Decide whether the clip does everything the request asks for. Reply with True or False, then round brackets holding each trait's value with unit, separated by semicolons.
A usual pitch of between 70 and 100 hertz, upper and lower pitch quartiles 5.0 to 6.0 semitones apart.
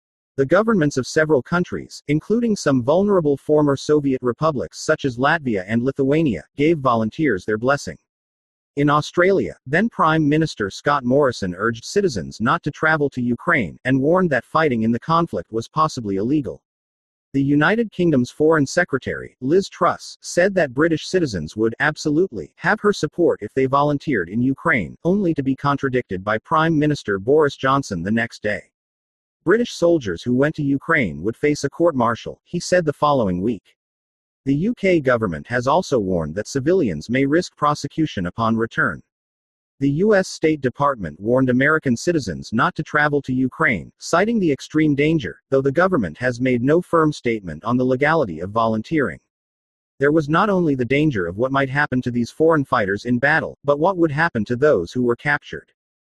False (140 Hz; 5.5 semitones)